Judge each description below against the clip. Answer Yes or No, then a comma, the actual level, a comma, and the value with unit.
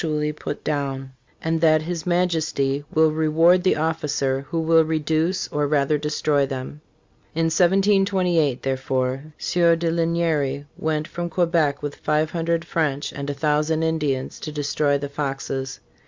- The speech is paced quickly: No, average, 145 wpm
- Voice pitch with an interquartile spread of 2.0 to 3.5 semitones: Yes, narrow, 2.6 semitones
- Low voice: No, medium, 155 Hz